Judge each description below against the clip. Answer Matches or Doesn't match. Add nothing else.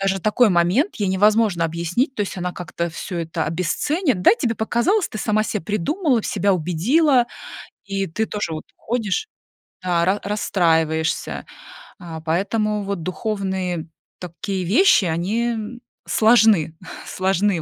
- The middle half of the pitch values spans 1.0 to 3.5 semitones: Doesn't match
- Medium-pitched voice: Doesn't match